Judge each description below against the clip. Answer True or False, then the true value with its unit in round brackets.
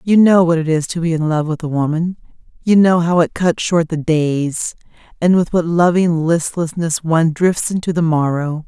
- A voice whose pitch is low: False (165 Hz)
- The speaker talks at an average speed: False (210 wpm)